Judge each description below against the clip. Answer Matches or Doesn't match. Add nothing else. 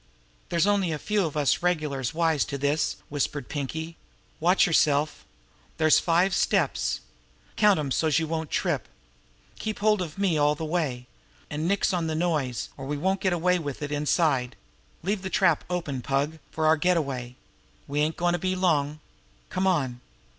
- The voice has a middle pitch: Matches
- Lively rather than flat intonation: Doesn't match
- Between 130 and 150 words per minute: Doesn't match